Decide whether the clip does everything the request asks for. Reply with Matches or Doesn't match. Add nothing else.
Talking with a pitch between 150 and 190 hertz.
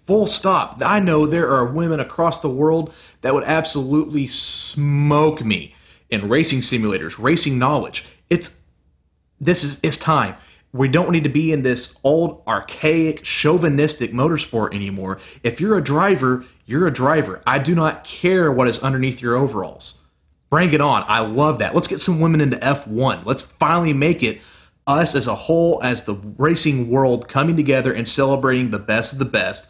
Doesn't match